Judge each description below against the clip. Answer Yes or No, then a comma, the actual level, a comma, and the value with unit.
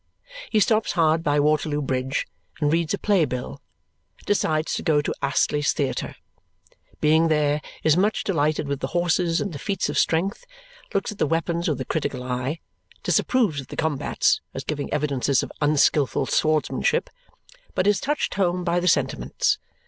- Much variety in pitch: No, average, 3.5 semitones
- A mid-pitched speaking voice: Yes, medium, 155 Hz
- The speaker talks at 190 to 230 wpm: No, average, 165 wpm